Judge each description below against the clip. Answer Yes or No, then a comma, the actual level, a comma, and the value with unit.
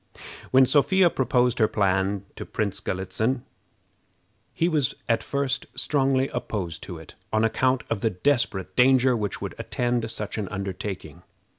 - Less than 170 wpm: Yes, average, 145 wpm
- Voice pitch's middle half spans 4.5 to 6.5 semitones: Yes, average, 4.9 semitones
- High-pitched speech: No, low, 115 Hz